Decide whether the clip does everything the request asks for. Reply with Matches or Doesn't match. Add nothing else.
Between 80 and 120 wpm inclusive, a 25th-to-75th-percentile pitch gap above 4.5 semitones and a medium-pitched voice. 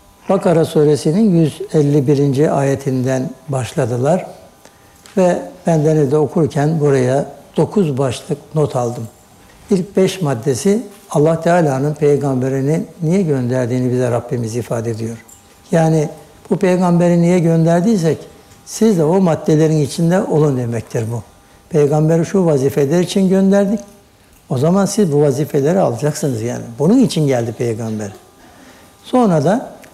Matches